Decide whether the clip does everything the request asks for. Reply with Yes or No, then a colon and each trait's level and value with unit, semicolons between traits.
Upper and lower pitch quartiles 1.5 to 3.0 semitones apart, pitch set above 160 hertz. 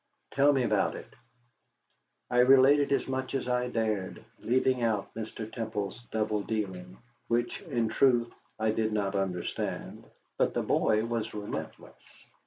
No: average, 2.7 semitones; low, 110 Hz